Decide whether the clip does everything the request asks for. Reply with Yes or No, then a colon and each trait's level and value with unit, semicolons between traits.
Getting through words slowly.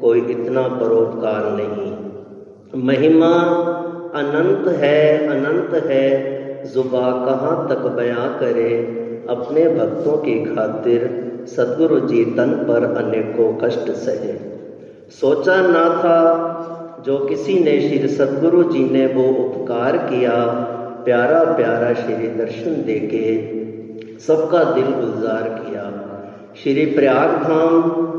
Yes: slow, 105 wpm